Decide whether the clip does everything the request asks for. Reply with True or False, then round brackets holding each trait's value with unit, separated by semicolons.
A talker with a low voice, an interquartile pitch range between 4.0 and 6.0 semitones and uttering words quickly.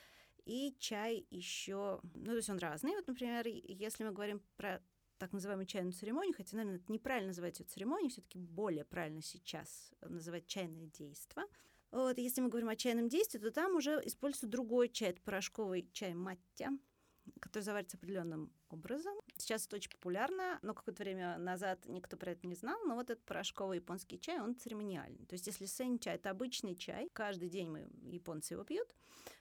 False (205 Hz; 5.2 semitones; 180 wpm)